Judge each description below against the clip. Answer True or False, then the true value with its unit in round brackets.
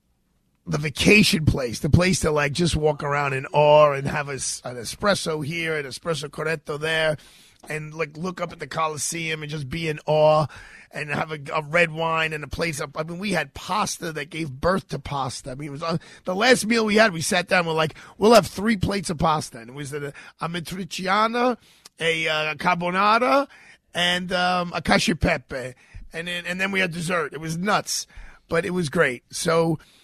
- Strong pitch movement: False (2.9 semitones)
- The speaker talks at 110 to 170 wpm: False (205 wpm)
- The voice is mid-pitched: True (165 Hz)